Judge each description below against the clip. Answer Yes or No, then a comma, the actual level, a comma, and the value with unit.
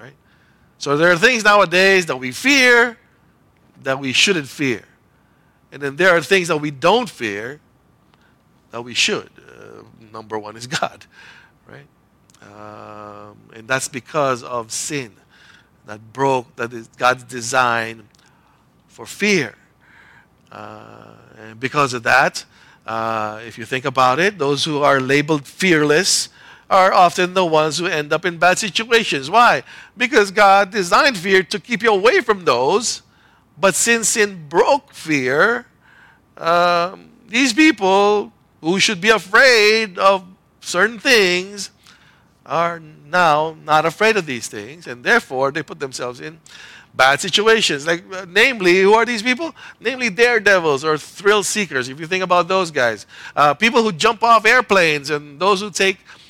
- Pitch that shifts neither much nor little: No, wide, 7.7 semitones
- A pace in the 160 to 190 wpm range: No, average, 150 wpm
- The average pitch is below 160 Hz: No, medium, 175 Hz